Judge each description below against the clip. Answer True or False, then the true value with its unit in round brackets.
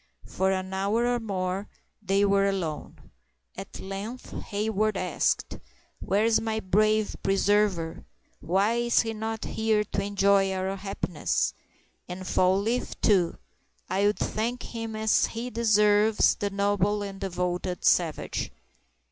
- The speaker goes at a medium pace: False (130 wpm)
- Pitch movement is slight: True (2.3 semitones)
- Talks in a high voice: True (200 Hz)